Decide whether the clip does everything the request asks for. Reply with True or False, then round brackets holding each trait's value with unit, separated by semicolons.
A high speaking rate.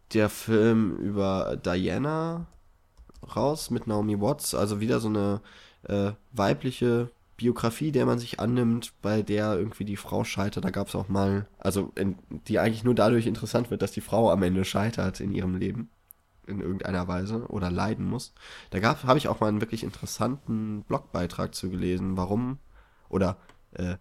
False (170 wpm)